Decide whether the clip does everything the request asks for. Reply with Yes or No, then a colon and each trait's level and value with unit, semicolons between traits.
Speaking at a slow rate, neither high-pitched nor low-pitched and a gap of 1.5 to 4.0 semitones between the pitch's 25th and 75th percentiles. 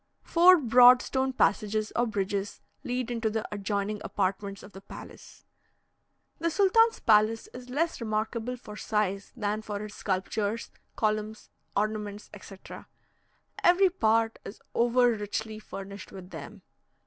No: slow, 130 wpm; high, 215 Hz; average, 3.2 semitones